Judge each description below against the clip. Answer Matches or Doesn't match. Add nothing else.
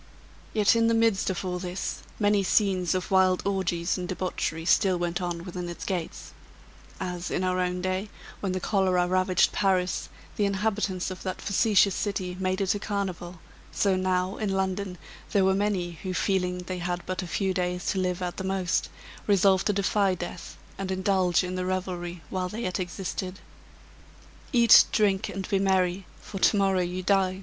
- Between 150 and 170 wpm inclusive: Doesn't match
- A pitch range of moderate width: Doesn't match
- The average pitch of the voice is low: Doesn't match